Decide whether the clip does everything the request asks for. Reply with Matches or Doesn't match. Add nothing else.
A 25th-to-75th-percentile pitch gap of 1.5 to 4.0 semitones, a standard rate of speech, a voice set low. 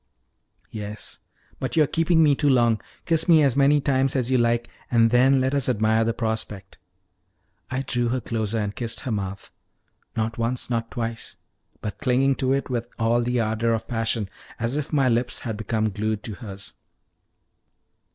Matches